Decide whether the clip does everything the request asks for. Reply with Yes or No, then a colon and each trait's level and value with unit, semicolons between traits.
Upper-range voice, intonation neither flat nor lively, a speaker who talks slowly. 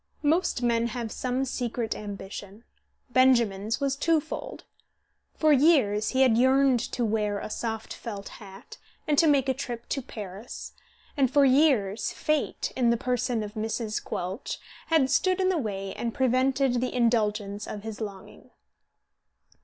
No: high, 240 Hz; average, 4.1 semitones; average, 150 wpm